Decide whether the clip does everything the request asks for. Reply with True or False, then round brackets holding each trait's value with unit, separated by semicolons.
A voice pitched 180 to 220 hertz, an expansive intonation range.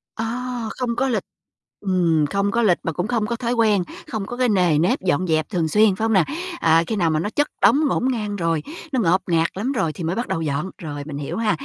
True (200 Hz; 5.7 semitones)